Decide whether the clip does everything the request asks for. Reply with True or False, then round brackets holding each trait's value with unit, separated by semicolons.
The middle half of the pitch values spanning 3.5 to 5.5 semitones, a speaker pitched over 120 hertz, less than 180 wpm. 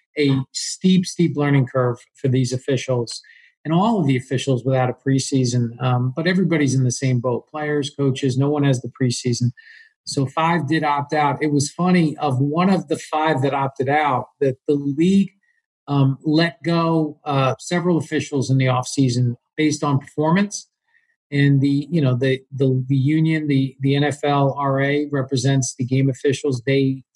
False (3.0 semitones; 140 Hz; 170 wpm)